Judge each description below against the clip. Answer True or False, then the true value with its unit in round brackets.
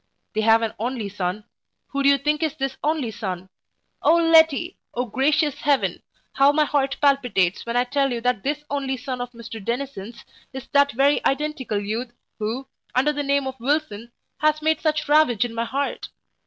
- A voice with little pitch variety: False (4.0 semitones)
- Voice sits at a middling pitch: False (265 Hz)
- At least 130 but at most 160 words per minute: False (185 wpm)